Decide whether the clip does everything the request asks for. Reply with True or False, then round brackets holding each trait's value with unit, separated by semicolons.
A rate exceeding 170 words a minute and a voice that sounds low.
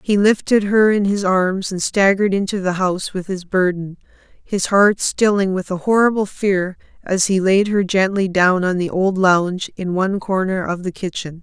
False (195 wpm; 190 Hz)